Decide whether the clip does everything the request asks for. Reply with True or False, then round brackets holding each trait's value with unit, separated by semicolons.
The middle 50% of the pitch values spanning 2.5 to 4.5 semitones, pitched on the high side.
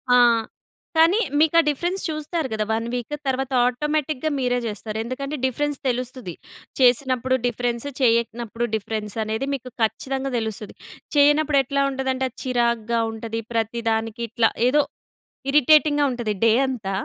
True (3.6 semitones; 250 Hz)